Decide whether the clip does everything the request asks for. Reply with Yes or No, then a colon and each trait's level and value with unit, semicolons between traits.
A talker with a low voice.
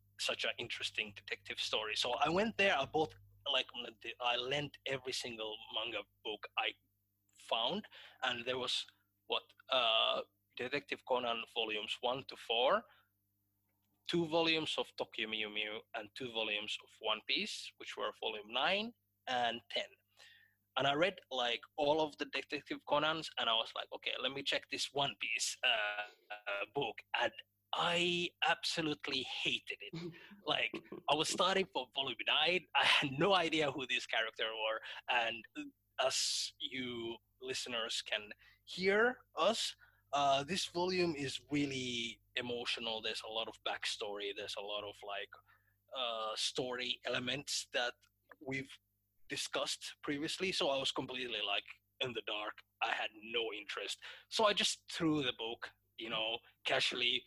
Yes: low, 125 Hz